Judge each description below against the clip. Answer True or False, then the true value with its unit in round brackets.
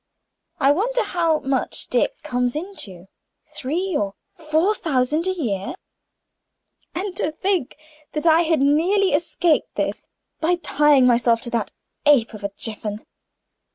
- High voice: True (300 Hz)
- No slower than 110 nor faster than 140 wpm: True (135 wpm)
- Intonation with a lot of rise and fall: True (5.9 semitones)